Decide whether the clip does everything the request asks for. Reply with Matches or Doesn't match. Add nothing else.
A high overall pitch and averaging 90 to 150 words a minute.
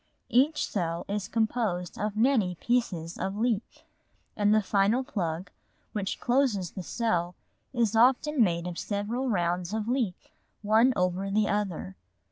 Matches